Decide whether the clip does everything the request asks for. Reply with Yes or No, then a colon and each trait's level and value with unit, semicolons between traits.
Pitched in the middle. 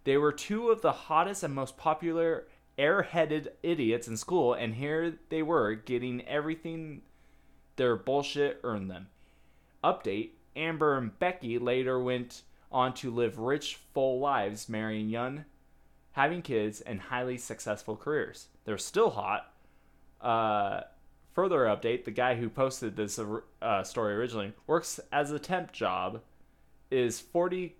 No: low, 125 Hz